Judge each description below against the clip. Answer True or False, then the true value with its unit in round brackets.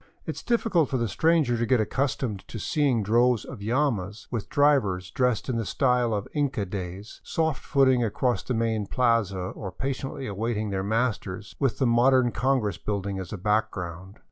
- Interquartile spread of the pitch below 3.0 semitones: False (4.5 semitones)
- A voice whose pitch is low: True (115 Hz)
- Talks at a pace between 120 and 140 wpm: False (175 wpm)